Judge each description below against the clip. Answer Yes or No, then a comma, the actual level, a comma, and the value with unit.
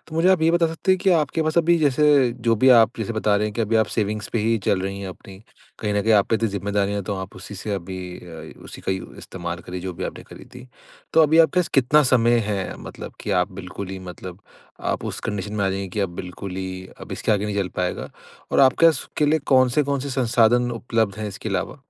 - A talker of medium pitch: No, low, 110 Hz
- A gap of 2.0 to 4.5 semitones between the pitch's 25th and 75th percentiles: No, average, 5.2 semitones